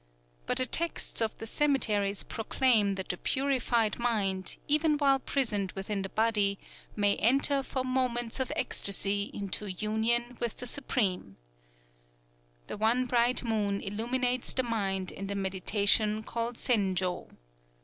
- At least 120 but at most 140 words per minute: Yes, slow, 135 wpm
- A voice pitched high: Yes, high, 225 Hz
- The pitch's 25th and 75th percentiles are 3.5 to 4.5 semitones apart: Yes, average, 3.9 semitones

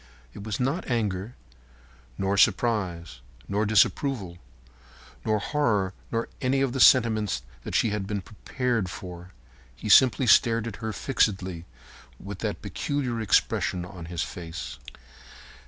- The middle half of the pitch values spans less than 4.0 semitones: No, average, 4.4 semitones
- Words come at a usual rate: No, slow, 130 wpm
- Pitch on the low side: Yes, low, 105 Hz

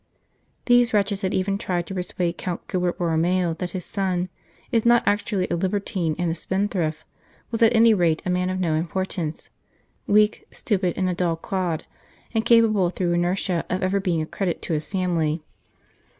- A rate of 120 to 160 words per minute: No, average, 175 wpm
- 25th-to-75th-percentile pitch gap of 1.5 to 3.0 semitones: Yes, narrow, 2.6 semitones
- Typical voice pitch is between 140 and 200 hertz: Yes, medium, 185 Hz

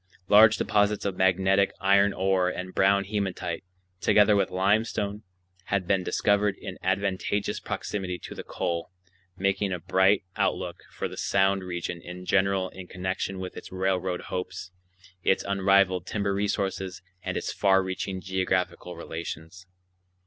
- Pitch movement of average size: No, narrow, 1.3 semitones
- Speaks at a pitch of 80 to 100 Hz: Yes, very low, 95 Hz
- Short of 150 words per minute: Yes, average, 140 wpm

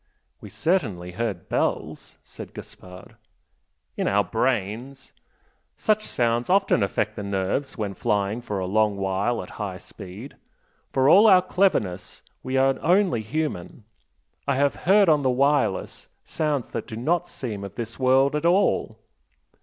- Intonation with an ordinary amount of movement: No, wide, 6.9 semitones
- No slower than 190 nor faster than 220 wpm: No, average, 145 wpm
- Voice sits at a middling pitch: No, low, 120 Hz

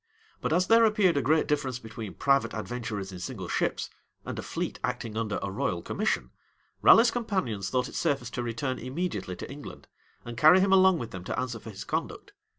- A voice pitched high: No, low, 125 Hz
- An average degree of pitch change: No, wide, 7.1 semitones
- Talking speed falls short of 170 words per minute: No, average, 200 wpm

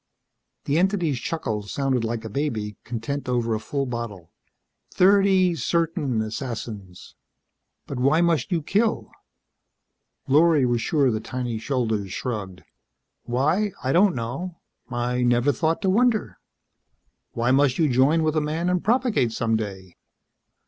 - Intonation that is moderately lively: No, wide, 6.3 semitones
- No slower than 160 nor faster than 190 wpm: No, slow, 135 wpm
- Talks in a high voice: No, low, 130 Hz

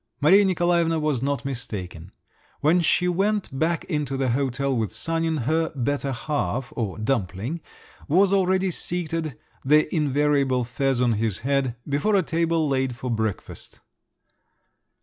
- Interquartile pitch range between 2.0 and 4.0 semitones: No, average, 4.8 semitones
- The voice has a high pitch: No, medium, 140 Hz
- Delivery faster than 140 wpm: No, slow, 135 wpm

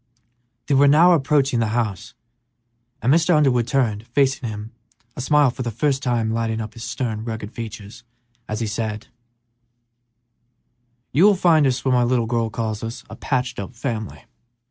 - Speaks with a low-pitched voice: Yes, low, 120 Hz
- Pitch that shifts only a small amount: No, average, 3.5 semitones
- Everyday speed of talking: Yes, average, 165 wpm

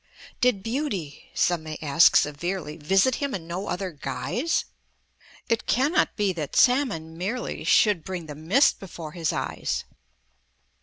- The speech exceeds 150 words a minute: No, average, 140 wpm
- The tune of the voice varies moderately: No, wide, 6.5 semitones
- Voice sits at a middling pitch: Yes, medium, 180 Hz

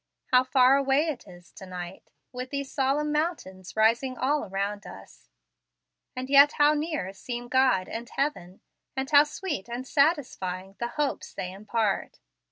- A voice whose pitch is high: Yes, very high, 255 Hz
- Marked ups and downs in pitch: Yes, wide, 6.5 semitones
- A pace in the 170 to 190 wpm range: No, average, 155 wpm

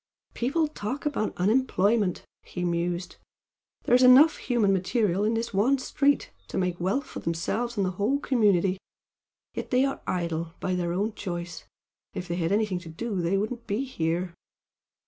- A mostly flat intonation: No, wide, 5.4 semitones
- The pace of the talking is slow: No, average, 165 wpm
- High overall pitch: Yes, high, 200 Hz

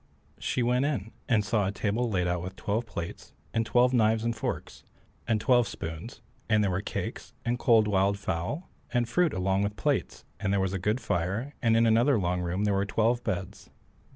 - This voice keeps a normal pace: No, fast, 210 wpm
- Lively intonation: No, average, 3.6 semitones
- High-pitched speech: No, low, 105 Hz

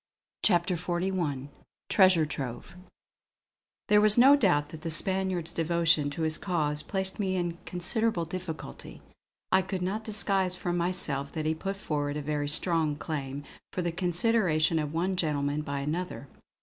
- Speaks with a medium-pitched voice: Yes, medium, 170 Hz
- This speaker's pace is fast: No, average, 155 wpm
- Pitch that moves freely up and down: No, average, 3.7 semitones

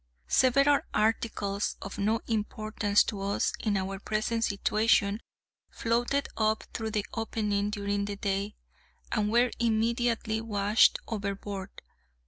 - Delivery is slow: Yes, slow, 115 wpm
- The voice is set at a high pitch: Yes, high, 215 Hz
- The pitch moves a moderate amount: No, narrow, 2.1 semitones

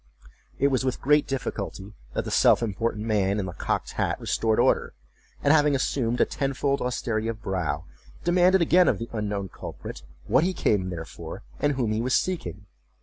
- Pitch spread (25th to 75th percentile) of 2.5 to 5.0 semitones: No, wide, 5.4 semitones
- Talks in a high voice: No, low, 115 Hz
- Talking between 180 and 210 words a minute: Yes, average, 185 wpm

